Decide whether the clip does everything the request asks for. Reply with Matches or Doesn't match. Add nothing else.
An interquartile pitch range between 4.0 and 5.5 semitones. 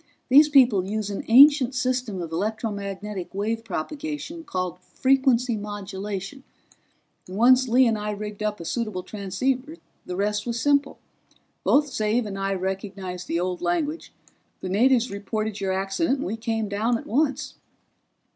Matches